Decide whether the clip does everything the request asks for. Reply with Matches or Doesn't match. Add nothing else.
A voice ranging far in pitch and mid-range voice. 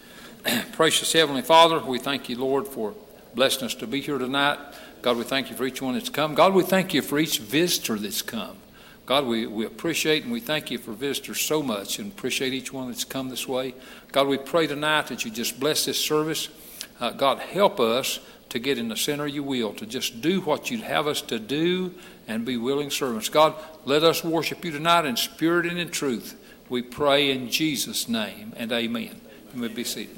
Doesn't match